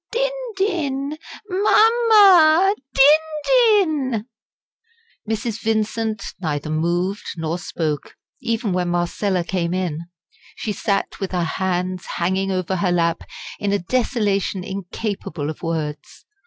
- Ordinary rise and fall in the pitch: No, wide, 7.7 semitones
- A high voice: Yes, high, 200 Hz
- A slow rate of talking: Yes, slow, 115 wpm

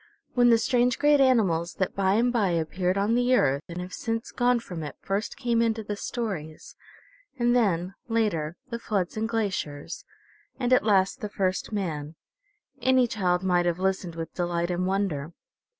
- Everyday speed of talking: Yes, average, 175 wpm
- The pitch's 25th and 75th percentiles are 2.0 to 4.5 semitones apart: No, average, 5.0 semitones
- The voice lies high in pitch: Yes, high, 195 Hz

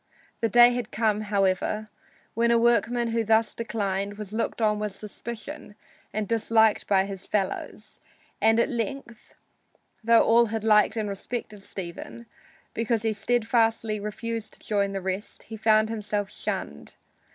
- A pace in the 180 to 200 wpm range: No, average, 150 wpm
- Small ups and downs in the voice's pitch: Yes, narrow, 1.9 semitones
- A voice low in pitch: No, high, 220 Hz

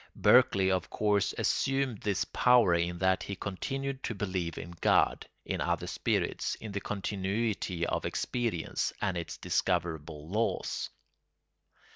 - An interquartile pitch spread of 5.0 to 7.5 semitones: No, average, 4.0 semitones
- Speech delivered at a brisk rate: No, slow, 135 wpm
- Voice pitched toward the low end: Yes, very low, 95 Hz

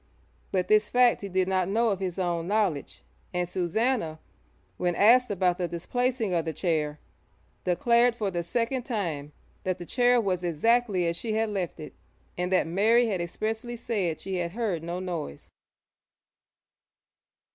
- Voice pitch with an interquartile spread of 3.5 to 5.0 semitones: Yes, average, 4.7 semitones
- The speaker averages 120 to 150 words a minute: No, average, 160 wpm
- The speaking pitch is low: No, medium, 185 Hz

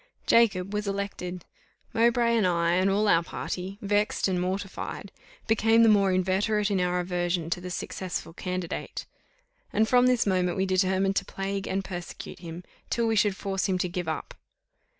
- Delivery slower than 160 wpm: No, average, 170 wpm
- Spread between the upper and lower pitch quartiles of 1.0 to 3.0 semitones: Yes, narrow, 2.4 semitones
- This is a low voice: No, high, 190 Hz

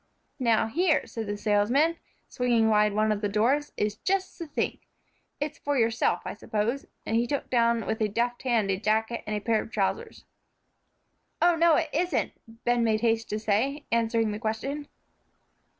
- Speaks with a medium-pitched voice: No, high, 230 Hz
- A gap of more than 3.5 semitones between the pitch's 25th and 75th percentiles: Yes, average, 4.5 semitones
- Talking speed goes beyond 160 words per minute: Yes, average, 180 wpm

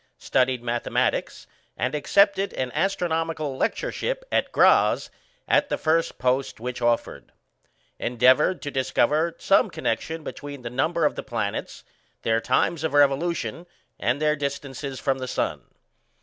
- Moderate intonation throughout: Yes, average, 4.4 semitones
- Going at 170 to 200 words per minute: No, slow, 135 wpm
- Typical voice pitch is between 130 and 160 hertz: Yes, medium, 140 Hz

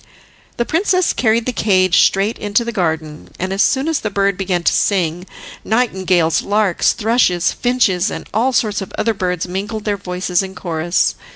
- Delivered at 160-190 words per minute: Yes, average, 175 wpm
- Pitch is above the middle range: Yes, high, 195 Hz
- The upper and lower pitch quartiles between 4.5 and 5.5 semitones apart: No, average, 3.7 semitones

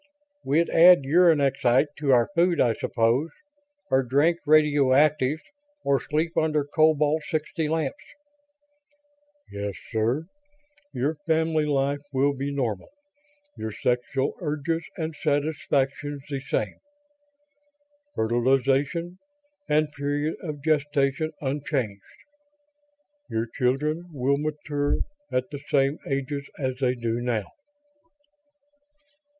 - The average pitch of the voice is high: No, medium, 145 Hz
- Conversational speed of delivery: No, slow, 100 wpm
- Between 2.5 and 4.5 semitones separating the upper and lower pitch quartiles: Yes, average, 2.8 semitones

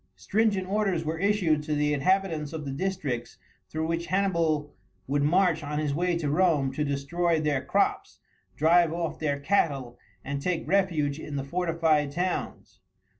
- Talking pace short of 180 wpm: Yes, average, 160 wpm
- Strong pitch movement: No, average, 3.7 semitones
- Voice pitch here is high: No, medium, 160 Hz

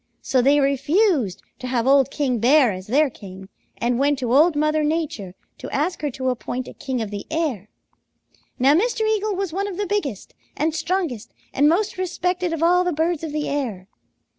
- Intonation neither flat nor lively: No, wide, 5.7 semitones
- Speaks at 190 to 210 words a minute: Yes, average, 195 wpm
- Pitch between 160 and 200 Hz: No, very high, 290 Hz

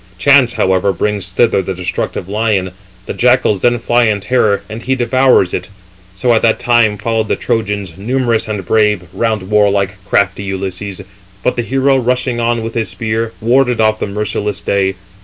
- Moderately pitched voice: No, low, 110 Hz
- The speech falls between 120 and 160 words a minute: No, average, 170 wpm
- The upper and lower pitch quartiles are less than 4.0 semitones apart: Yes, average, 3.2 semitones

